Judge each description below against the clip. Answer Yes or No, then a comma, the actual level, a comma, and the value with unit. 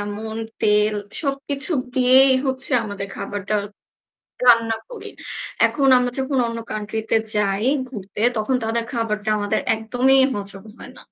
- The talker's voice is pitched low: No, high, 225 Hz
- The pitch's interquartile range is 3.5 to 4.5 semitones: Yes, average, 3.9 semitones